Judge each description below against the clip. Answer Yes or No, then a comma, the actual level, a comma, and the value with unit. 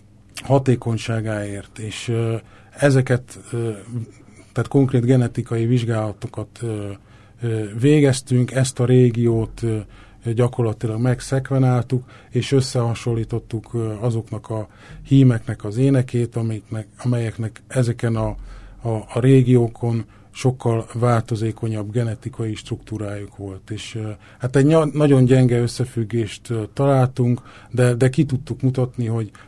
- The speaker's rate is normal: No, slow, 90 wpm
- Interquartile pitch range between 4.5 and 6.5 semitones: No, narrow, 2.5 semitones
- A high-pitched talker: No, low, 115 Hz